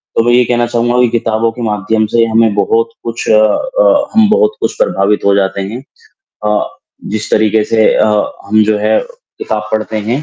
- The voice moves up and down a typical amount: No, narrow, 2.0 semitones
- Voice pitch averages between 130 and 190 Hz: No, low, 115 Hz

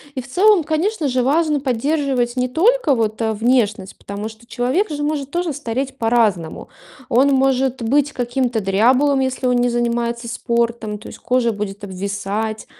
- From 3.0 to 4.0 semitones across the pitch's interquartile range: Yes, average, 3.7 semitones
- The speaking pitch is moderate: No, high, 245 Hz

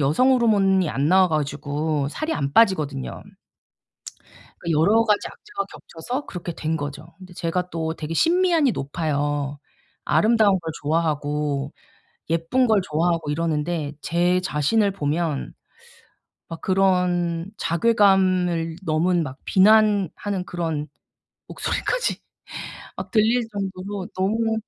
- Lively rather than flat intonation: No, average, 4.6 semitones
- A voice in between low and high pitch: Yes, medium, 175 Hz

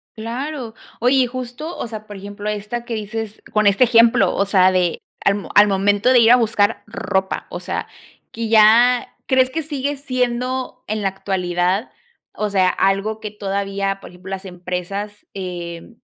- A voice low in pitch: No, high, 210 Hz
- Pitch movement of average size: Yes, average, 3.6 semitones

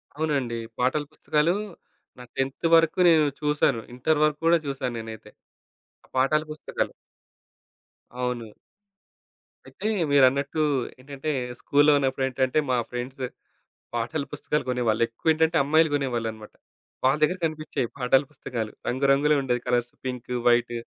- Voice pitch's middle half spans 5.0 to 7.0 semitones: No, average, 3.5 semitones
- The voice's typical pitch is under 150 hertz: Yes, low, 135 Hz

